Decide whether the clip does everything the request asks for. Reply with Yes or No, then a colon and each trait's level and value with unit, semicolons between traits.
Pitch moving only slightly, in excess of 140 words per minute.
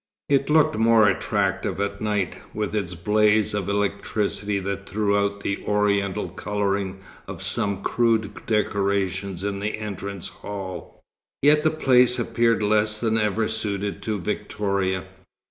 No: narrow, 1.6 semitones; slow, 135 wpm